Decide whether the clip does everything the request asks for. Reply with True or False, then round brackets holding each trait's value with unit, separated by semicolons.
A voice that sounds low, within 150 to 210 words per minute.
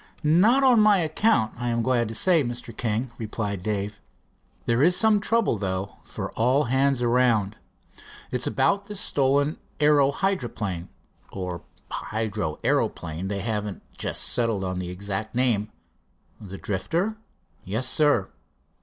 False (120 Hz; 135 wpm)